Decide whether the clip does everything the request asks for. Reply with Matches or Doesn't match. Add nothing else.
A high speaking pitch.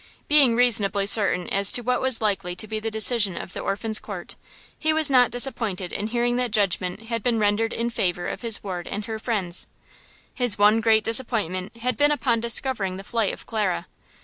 Matches